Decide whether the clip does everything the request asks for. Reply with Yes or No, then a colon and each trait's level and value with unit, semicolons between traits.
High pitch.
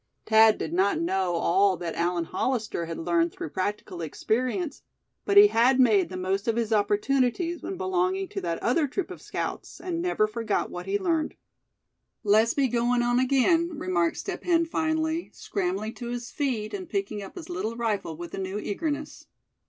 Yes: high, 230 Hz